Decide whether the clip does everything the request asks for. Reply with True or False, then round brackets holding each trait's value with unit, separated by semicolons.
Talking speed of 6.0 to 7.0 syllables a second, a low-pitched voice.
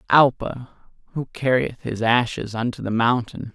False (4.6 syllables/s; 120 Hz)